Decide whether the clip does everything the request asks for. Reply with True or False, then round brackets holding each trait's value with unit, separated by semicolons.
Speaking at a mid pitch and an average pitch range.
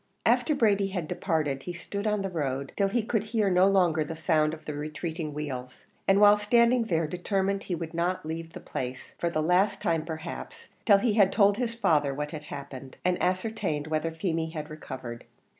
True (170 Hz; 4.5 semitones)